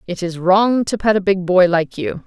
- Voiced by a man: No, female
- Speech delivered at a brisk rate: Yes, fast, 265 wpm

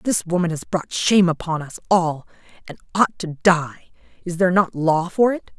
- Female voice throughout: Yes, female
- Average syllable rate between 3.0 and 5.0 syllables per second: Yes, 4.9 syllables/s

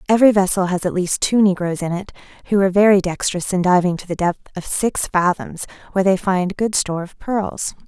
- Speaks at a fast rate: Yes, fast, 215 wpm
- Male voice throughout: No, female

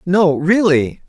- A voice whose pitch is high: No, medium, 175 Hz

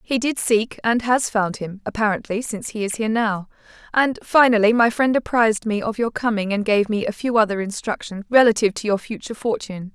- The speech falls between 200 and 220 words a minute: Yes, fast, 205 wpm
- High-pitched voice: Yes, high, 220 Hz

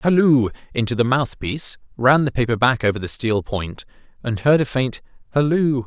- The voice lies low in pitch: Yes, low, 125 Hz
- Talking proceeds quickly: No, average, 175 wpm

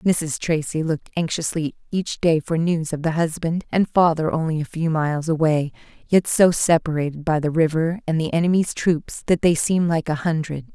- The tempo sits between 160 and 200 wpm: Yes, average, 190 wpm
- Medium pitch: Yes, medium, 160 Hz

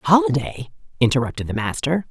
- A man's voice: No, female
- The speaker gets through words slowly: Yes, slow, 115 wpm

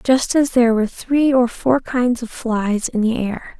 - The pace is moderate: No, fast, 215 wpm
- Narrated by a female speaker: Yes, female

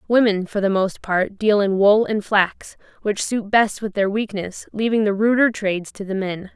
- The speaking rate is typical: No, fast, 210 wpm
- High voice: Yes, high, 205 Hz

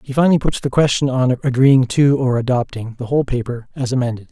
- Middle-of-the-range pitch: No, low, 130 Hz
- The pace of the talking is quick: Yes, fast, 210 wpm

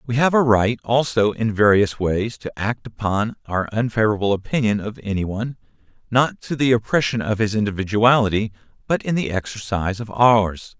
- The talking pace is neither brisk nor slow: Yes, average, 165 wpm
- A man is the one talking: Yes, male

